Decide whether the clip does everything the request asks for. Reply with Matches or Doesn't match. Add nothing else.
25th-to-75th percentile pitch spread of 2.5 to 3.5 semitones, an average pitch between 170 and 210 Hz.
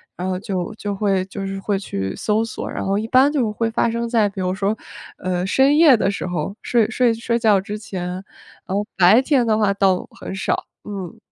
Matches